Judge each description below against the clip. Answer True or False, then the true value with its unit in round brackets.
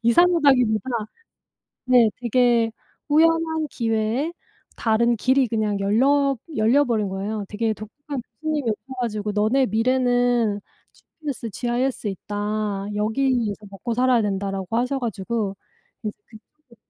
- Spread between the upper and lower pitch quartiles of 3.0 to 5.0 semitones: True (3.5 semitones)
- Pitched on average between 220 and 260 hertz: True (235 Hz)